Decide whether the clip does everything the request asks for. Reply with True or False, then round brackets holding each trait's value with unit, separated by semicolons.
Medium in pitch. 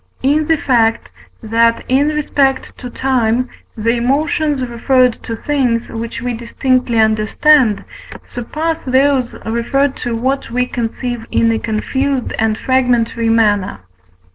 False (245 Hz)